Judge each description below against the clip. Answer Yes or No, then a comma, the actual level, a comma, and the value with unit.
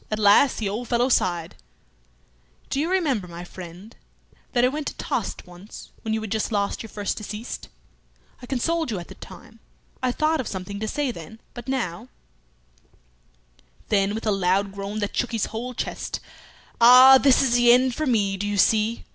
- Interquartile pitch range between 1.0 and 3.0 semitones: No, average, 4.2 semitones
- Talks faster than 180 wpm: Yes, average, 190 wpm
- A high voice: Yes, high, 220 Hz